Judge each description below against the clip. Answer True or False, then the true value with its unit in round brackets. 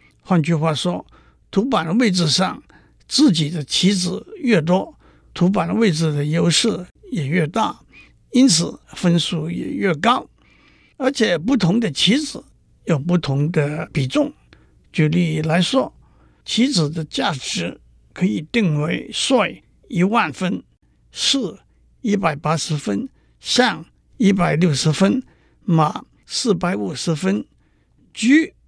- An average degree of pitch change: False (5.8 semitones)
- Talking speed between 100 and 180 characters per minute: True (175 characters per minute)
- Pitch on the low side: False (180 Hz)